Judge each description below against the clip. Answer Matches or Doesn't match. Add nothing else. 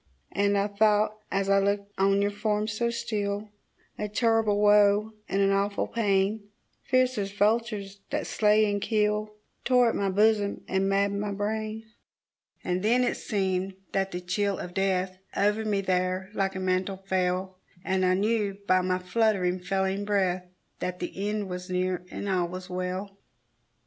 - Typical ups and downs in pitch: Doesn't match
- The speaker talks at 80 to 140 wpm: Doesn't match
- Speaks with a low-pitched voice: Doesn't match